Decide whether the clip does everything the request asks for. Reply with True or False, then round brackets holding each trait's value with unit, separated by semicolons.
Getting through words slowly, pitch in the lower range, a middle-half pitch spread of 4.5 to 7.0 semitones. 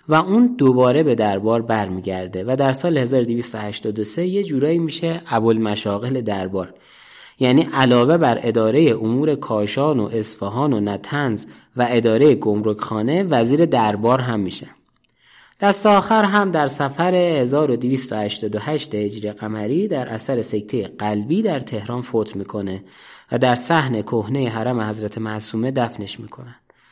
True (130 wpm; 120 Hz; 5.3 semitones)